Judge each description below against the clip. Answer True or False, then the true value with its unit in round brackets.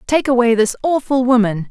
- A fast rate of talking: False (175 wpm)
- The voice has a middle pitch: False (240 Hz)